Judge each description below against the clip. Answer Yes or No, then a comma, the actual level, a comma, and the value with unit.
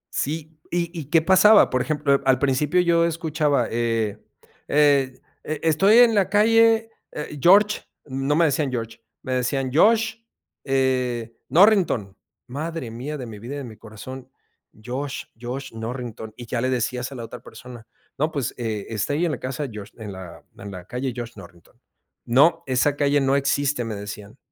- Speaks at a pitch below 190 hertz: Yes, low, 135 Hz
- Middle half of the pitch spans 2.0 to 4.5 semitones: No, average, 4.9 semitones